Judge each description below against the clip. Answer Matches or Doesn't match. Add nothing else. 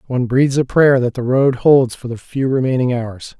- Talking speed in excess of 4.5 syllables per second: Matches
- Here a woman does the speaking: Doesn't match